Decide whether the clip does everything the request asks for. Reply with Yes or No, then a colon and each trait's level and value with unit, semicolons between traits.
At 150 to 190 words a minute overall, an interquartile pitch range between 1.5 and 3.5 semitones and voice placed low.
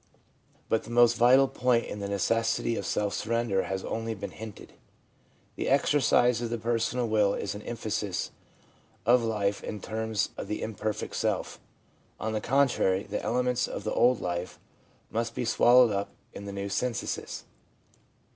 Yes: average, 165 wpm; average, 2.7 semitones; low, 110 Hz